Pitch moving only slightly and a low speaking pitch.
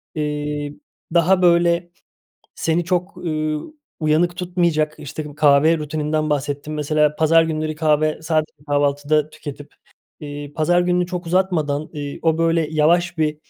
No: narrow, 2.3 semitones; medium, 155 Hz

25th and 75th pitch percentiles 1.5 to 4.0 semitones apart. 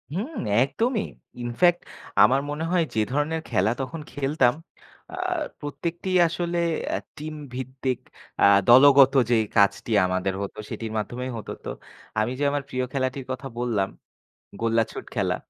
No: average, 4.8 semitones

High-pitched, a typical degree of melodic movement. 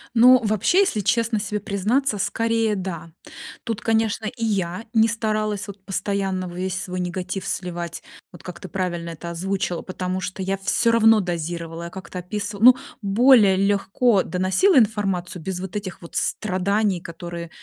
Yes: high, 195 Hz; average, 3.1 semitones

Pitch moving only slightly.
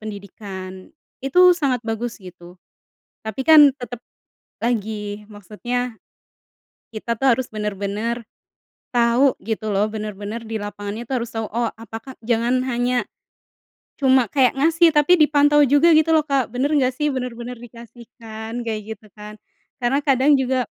No: average, 3.6 semitones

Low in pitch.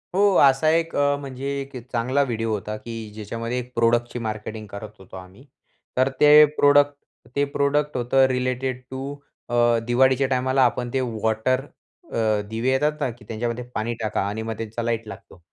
Yes: low, 120 Hz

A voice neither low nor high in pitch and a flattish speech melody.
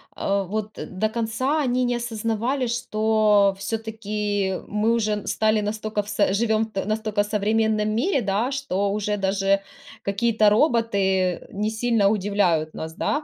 No: high, 215 Hz; narrow, 2.1 semitones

